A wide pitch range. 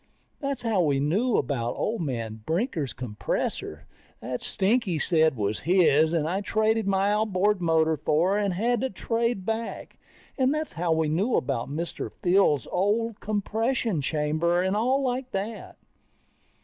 Yes: wide, 6.1 semitones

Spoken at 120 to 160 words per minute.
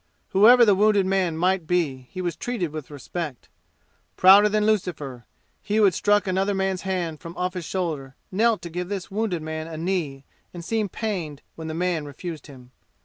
No: average, 190 wpm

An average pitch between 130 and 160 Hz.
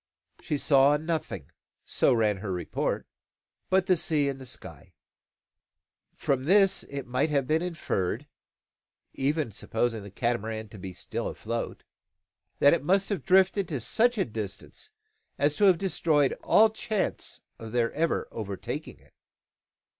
Yes: medium, 140 Hz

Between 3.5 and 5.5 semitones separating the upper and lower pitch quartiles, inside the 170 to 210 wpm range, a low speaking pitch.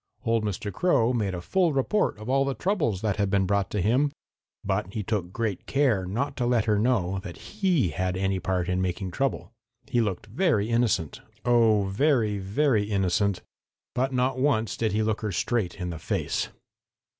Yes: average, 4.6 semitones; average, 190 wpm; low, 110 Hz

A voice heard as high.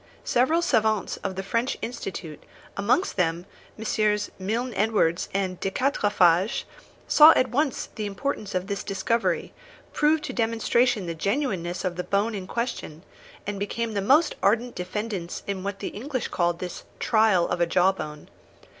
Yes: high, 205 Hz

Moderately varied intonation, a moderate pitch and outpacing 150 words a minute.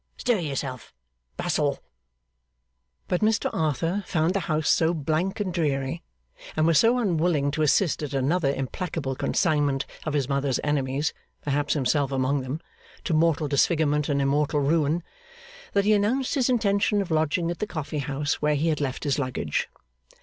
Yes: average, 3.7 semitones; medium, 155 Hz; average, 160 wpm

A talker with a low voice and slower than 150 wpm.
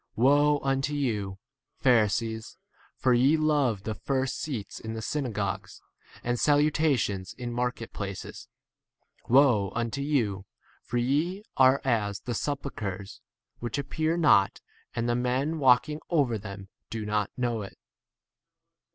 Yes: low, 125 Hz; average, 140 wpm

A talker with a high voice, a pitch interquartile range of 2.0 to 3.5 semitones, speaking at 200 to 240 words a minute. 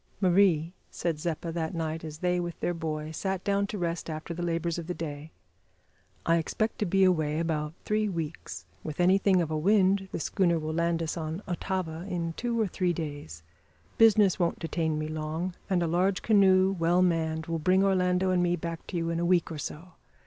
No: medium, 170 Hz; narrow, 2.6 semitones; fast, 205 wpm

